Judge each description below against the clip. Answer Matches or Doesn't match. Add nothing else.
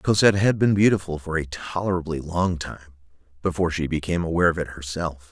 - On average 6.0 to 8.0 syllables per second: Matches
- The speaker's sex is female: Doesn't match